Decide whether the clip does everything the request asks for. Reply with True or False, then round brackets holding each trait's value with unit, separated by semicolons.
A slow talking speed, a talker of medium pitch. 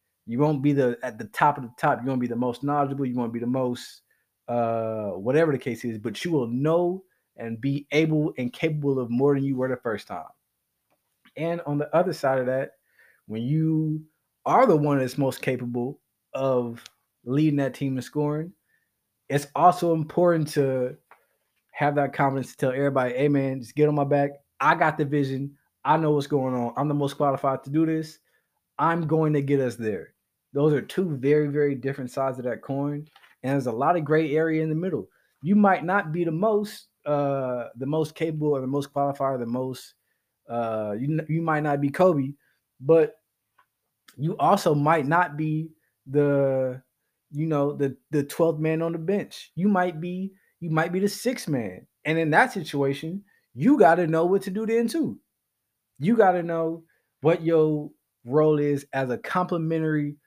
False (195 wpm; 145 Hz)